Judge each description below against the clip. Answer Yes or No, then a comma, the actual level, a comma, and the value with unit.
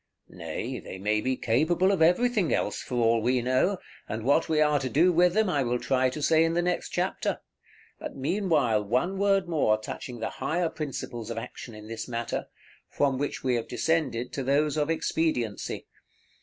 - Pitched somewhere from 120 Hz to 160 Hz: Yes, low, 135 Hz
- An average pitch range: No, wide, 5.7 semitones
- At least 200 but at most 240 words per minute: No, average, 190 wpm